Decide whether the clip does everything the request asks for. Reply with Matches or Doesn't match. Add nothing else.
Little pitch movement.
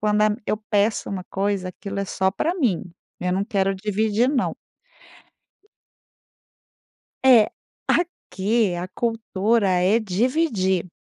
Doesn't match